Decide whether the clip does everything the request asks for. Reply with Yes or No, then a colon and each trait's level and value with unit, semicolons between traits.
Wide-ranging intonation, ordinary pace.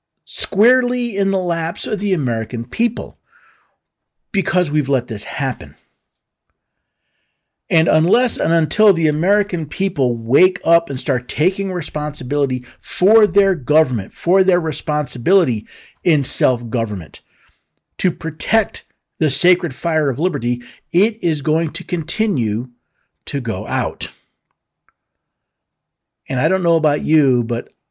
No: wide, 6.2 semitones; slow, 125 wpm